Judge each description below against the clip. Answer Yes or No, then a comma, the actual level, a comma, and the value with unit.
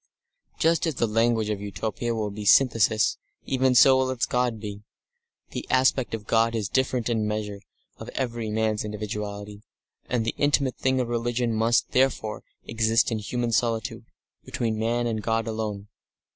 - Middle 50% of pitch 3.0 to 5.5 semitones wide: No, narrow, 2.4 semitones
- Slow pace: No, average, 170 wpm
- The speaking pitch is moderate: No, low, 115 Hz